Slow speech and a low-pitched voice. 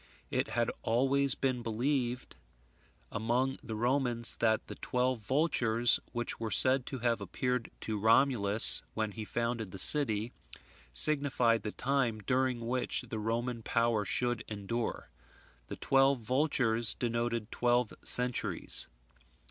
Yes: slow, 125 wpm; low, 120 Hz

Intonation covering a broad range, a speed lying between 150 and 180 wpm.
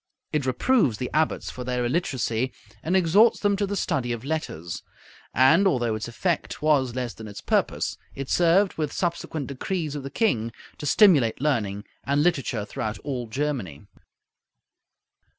Yes: wide, 5.7 semitones; average, 155 wpm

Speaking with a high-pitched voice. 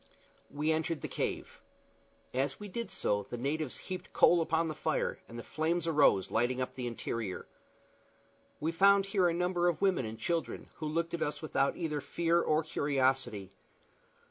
No: medium, 155 Hz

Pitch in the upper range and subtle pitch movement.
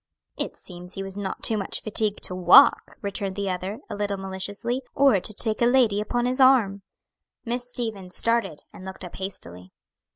No: high, 200 Hz; average, 3.8 semitones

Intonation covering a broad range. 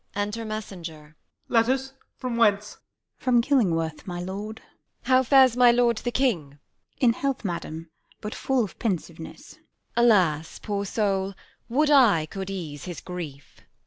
Yes: wide, 5.9 semitones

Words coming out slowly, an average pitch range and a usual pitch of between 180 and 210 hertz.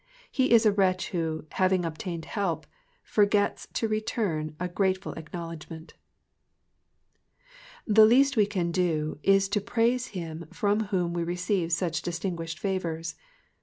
Yes: slow, 130 wpm; average, 3.8 semitones; medium, 185 Hz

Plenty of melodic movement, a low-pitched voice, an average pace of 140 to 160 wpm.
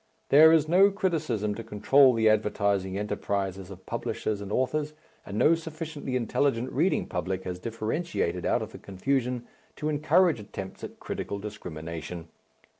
Yes: wide, 7.3 semitones; low, 115 Hz; average, 145 wpm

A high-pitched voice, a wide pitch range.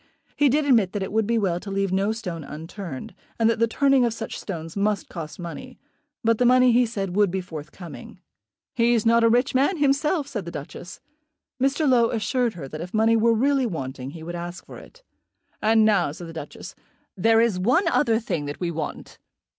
Yes: high, 215 Hz; wide, 5.7 semitones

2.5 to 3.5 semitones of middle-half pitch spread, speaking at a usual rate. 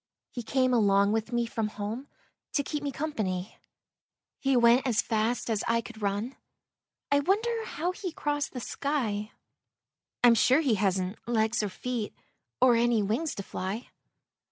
No: average, 4.4 semitones; average, 155 wpm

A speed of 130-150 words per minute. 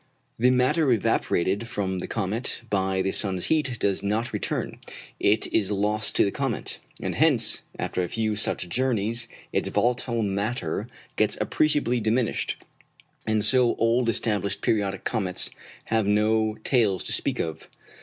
Yes: average, 145 wpm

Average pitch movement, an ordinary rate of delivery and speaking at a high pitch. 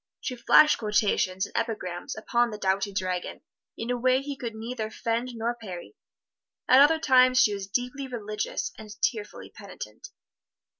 Yes: average, 3.4 semitones; average, 155 wpm; high, 230 Hz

